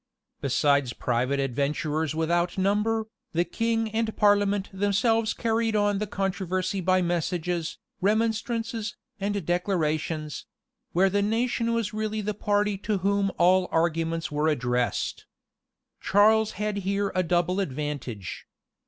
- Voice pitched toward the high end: Yes, high, 195 Hz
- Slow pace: Yes, slow, 120 wpm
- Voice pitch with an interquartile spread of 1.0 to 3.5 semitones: No, average, 4.5 semitones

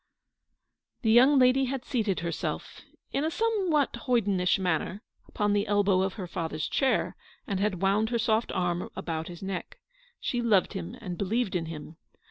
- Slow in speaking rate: No, average, 175 wpm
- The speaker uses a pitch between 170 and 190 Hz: No, high, 205 Hz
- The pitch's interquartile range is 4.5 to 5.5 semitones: Yes, average, 5.2 semitones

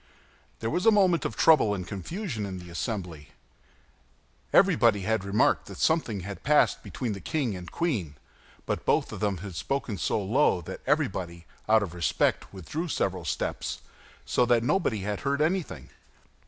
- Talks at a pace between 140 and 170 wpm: Yes, average, 165 wpm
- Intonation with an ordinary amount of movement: No, wide, 7.2 semitones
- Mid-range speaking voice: No, low, 105 Hz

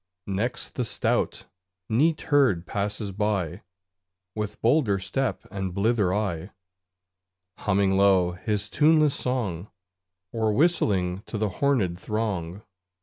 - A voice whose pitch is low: Yes, low, 105 Hz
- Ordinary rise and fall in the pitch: Yes, average, 4.0 semitones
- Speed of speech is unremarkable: No, slow, 110 wpm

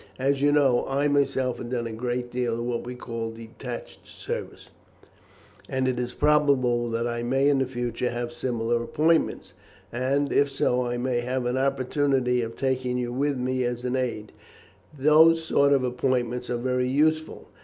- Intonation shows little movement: Yes, narrow, 2.2 semitones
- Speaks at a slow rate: No, average, 175 wpm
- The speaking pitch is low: Yes, low, 125 Hz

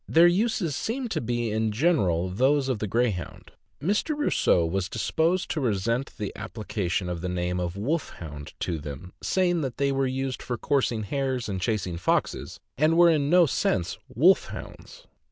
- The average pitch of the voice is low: Yes, low, 120 Hz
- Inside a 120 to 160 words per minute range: No, average, 170 wpm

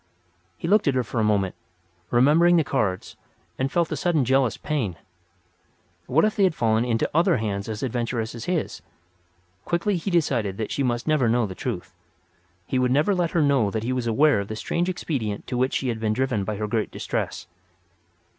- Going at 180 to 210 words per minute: Yes, average, 200 wpm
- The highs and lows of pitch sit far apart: Yes, wide, 5.9 semitones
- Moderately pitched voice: No, low, 125 Hz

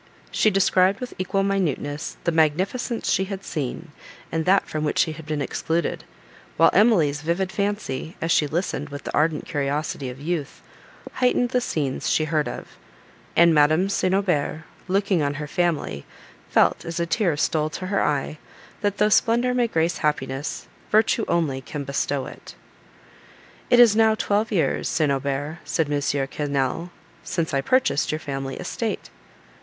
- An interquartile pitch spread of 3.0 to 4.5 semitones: No, average, 5.0 semitones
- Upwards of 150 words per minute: Yes, average, 160 wpm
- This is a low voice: No, medium, 160 Hz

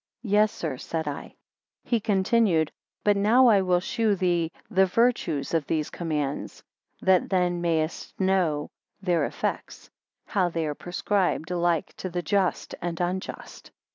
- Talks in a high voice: No, medium, 180 Hz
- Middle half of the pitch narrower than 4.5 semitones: Yes, average, 3.3 semitones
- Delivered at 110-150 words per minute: Yes, average, 145 wpm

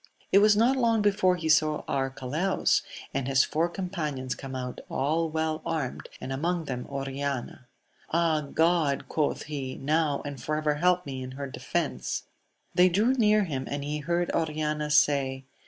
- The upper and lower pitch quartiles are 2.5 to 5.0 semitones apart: Yes, average, 4.1 semitones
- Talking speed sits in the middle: Yes, average, 165 wpm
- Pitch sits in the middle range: Yes, medium, 150 Hz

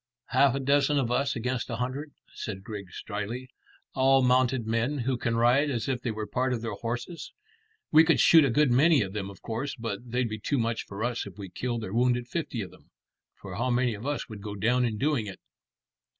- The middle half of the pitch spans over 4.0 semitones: No, average, 3.3 semitones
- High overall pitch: No, low, 120 Hz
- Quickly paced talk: Yes, fast, 225 wpm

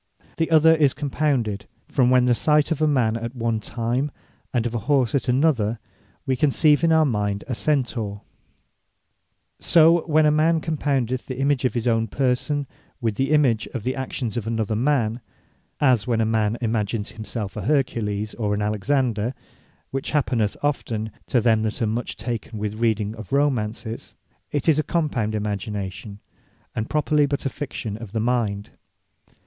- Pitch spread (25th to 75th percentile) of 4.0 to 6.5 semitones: Yes, average, 4.6 semitones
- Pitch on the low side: Yes, low, 120 Hz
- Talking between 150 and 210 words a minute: Yes, average, 175 wpm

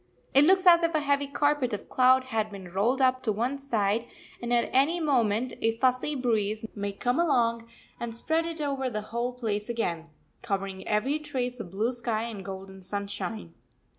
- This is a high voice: Yes, high, 235 Hz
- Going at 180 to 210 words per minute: Yes, average, 185 wpm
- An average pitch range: Yes, average, 4.5 semitones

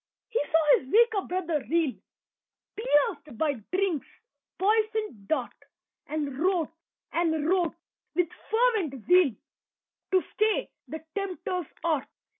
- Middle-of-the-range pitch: No, very high, 340 Hz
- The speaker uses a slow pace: Yes, slow, 110 wpm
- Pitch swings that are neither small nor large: Yes, average, 4.7 semitones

